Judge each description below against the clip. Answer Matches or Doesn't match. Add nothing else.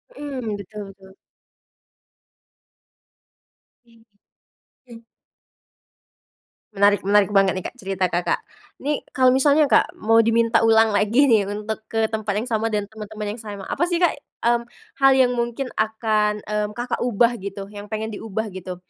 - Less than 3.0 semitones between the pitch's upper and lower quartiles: Matches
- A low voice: Doesn't match